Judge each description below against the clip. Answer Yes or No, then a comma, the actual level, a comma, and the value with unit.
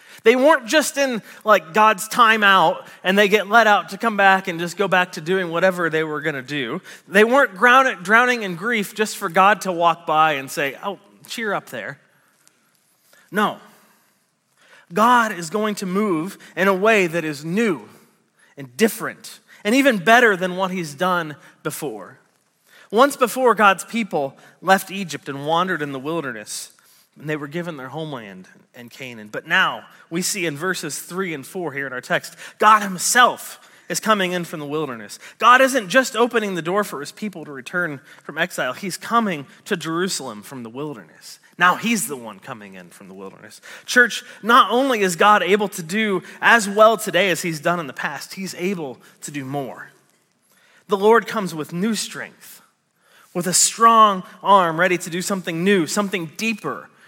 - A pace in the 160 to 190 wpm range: Yes, average, 185 wpm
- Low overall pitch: No, high, 190 Hz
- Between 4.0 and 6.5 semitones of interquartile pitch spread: Yes, average, 4.9 semitones